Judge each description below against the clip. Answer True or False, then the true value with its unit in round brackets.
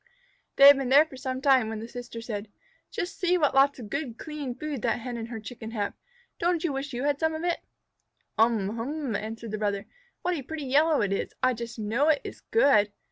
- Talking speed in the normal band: False (230 wpm)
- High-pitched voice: True (255 Hz)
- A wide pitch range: False (4.6 semitones)